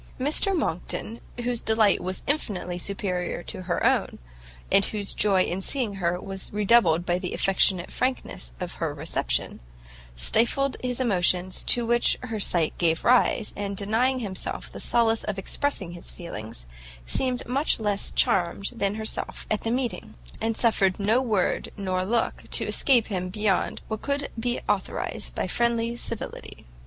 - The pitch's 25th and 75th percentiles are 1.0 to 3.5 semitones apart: No, average, 4.4 semitones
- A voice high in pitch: Yes, high, 210 Hz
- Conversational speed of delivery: Yes, average, 155 wpm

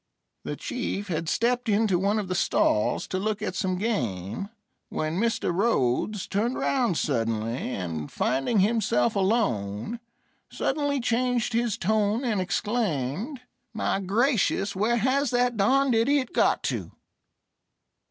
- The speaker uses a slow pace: Yes, slow, 130 wpm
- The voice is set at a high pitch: Yes, high, 210 Hz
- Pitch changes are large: Yes, wide, 5.8 semitones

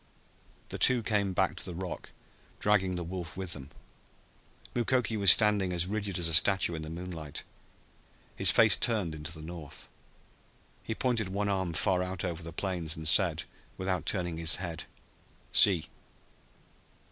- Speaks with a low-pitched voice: Yes, very low, 90 Hz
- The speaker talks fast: No, average, 160 wpm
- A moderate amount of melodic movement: Yes, average, 3.2 semitones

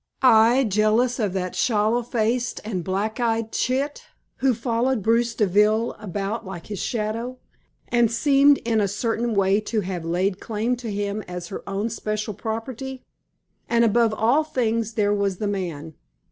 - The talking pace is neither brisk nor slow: Yes, average, 160 wpm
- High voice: Yes, high, 220 Hz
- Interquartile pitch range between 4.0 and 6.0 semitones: No, average, 2.8 semitones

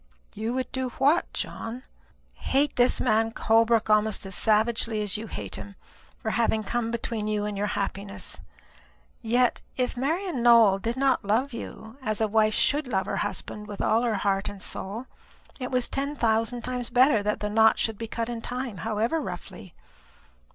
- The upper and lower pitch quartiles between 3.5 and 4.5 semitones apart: No, average, 2.9 semitones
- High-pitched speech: Yes, high, 225 Hz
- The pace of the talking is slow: No, average, 180 wpm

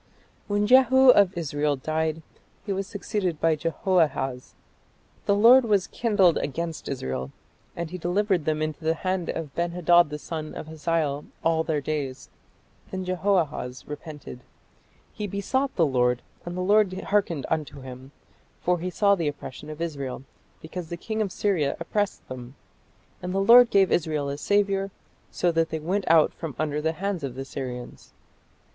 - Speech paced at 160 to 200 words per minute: Yes, average, 165 wpm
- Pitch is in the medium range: Yes, medium, 165 Hz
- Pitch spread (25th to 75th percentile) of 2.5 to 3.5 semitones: No, average, 4.7 semitones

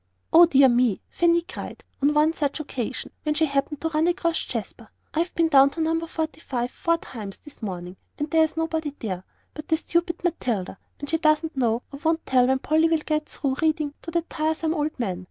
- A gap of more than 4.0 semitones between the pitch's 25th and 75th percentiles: No, average, 3.5 semitones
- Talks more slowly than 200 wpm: No, fast, 205 wpm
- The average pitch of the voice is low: No, very high, 305 Hz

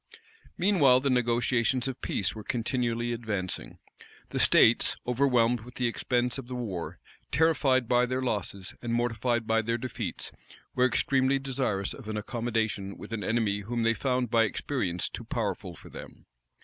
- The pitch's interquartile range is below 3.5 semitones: Yes, narrow, 2.4 semitones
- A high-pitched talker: No, low, 120 Hz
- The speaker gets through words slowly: No, average, 160 wpm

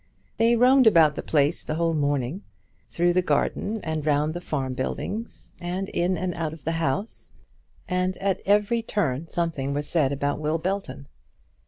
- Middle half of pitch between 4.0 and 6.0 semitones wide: Yes, average, 4.5 semitones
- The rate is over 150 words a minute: Yes, average, 170 wpm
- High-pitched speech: No, medium, 165 Hz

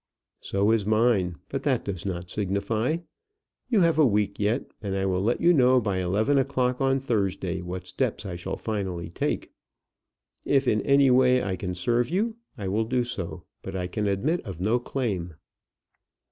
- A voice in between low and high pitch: No, low, 105 Hz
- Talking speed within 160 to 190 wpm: Yes, average, 175 wpm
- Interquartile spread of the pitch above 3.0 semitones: Yes, average, 5.1 semitones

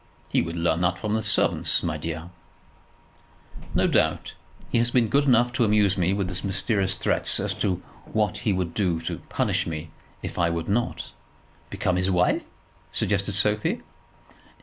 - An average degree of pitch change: Yes, average, 3.6 semitones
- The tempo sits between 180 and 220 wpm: No, average, 170 wpm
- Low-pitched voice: Yes, very low, 95 Hz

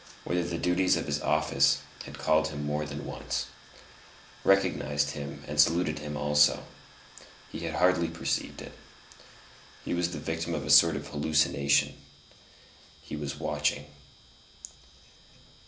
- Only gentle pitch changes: Yes, narrow, 2.1 semitones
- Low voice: Yes, very low, 75 Hz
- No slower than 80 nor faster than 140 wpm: Yes, slow, 135 wpm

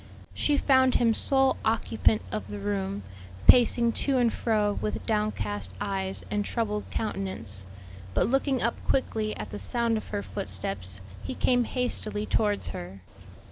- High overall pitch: Yes, high, 210 Hz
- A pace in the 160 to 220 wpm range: No, average, 145 wpm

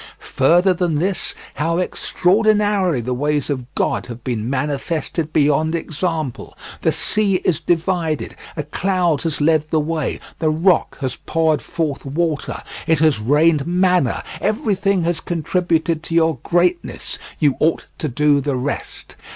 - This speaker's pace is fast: No, average, 145 wpm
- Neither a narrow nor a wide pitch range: Yes, average, 3.3 semitones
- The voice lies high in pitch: No, medium, 160 Hz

